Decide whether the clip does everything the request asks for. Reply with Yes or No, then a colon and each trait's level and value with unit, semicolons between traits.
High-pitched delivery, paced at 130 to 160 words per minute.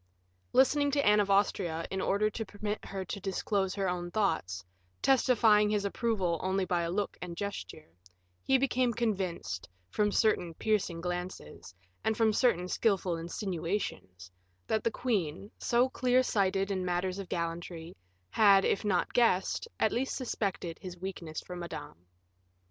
Yes: high, 195 Hz; average, 150 wpm